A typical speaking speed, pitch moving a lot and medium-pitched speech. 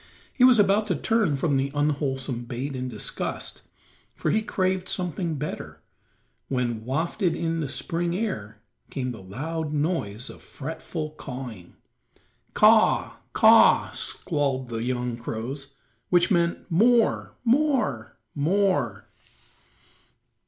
No: slow, 130 wpm; wide, 6.1 semitones; medium, 150 Hz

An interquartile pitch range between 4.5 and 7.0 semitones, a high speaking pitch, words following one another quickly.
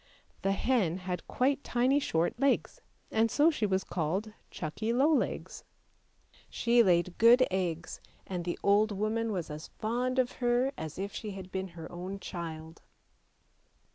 No: wide, 5.5 semitones; high, 200 Hz; average, 160 wpm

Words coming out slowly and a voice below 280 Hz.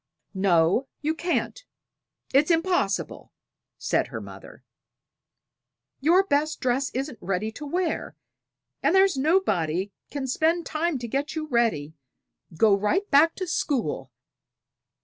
No: slow, 120 wpm; very high, 285 Hz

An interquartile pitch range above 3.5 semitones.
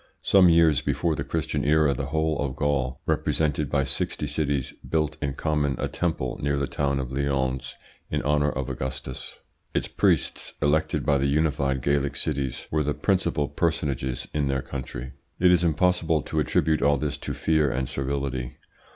No: narrow, 2.5 semitones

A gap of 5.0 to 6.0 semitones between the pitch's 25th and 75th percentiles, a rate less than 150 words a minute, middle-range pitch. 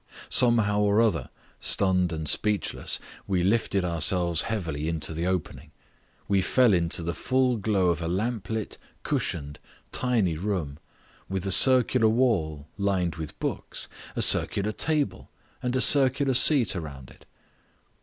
No: wide, 5.4 semitones; average, 140 wpm; very low, 95 Hz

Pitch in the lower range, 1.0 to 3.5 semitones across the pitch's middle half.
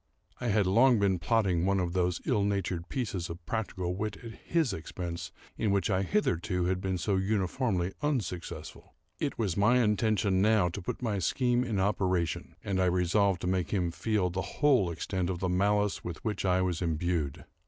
Yes: very low, 95 Hz; average, 3.1 semitones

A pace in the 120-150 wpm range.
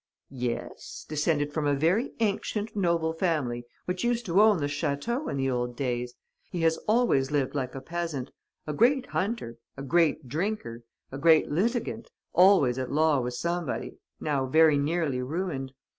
No: average, 160 wpm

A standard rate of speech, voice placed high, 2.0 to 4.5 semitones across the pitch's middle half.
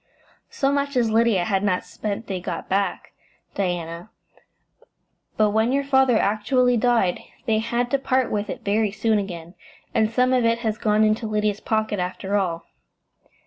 Yes: average, 165 wpm; high, 215 Hz; average, 3.1 semitones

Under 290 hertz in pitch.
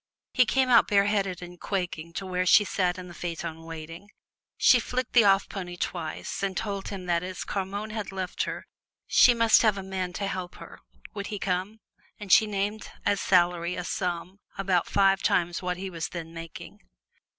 Yes: high, 190 Hz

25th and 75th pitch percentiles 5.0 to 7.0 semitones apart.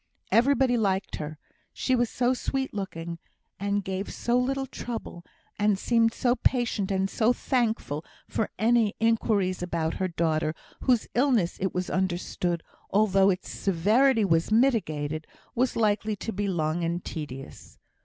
Yes: wide, 5.4 semitones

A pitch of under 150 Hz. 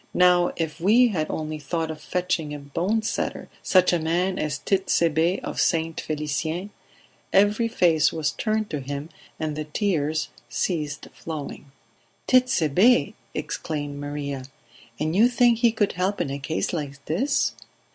No: medium, 165 Hz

